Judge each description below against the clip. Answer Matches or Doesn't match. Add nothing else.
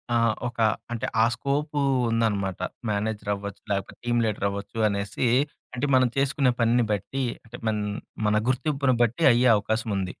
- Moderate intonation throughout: Matches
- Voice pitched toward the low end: Matches